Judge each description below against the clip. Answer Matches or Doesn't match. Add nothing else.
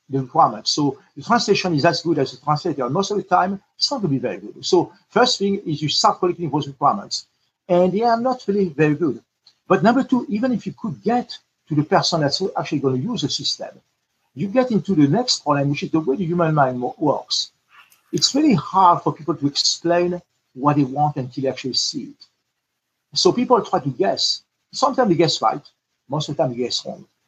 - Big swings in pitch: Matches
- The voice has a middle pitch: Matches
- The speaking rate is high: Matches